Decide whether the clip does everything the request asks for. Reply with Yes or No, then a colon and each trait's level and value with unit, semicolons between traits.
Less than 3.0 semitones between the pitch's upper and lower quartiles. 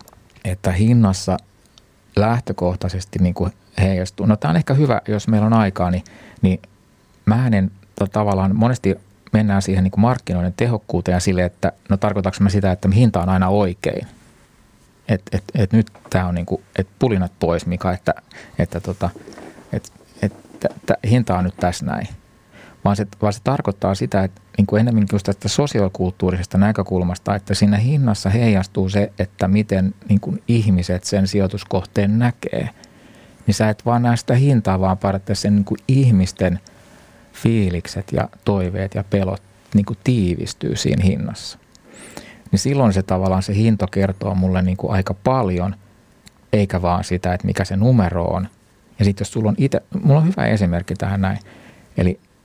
Yes: narrow, 2.5 semitones